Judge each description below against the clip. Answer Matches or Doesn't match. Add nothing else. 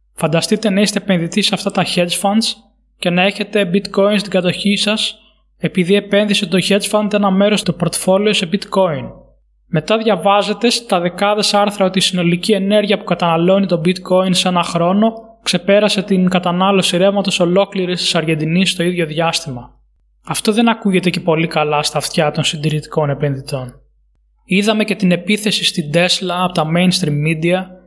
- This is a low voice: Doesn't match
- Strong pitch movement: Doesn't match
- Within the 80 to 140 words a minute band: Doesn't match